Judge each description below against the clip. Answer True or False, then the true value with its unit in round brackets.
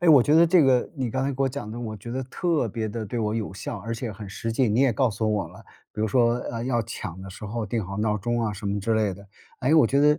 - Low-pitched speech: True (115 Hz)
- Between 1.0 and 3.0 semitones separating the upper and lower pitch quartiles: False (3.6 semitones)